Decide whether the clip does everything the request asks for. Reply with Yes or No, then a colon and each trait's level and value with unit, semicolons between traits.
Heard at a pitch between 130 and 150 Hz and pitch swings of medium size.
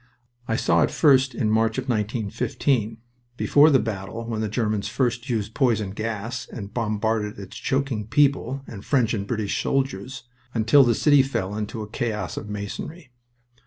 No: low, 115 Hz; average, 3.6 semitones